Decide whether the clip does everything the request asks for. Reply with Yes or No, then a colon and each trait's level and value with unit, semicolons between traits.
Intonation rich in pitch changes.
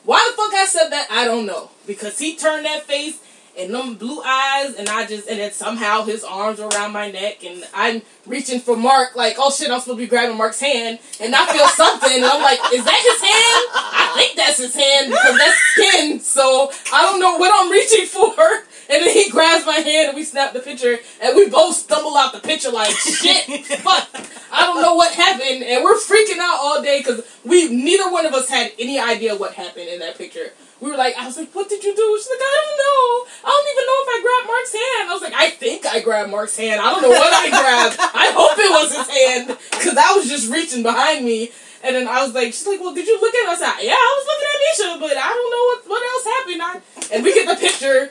Yes: wide, 7.7 semitones